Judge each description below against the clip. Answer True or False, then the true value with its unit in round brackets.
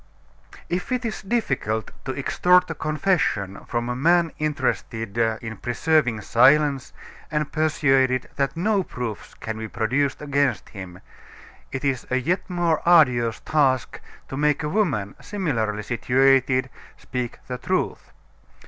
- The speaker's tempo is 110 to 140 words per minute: True (135 wpm)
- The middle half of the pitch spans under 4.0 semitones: False (5.0 semitones)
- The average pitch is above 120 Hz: True (135 Hz)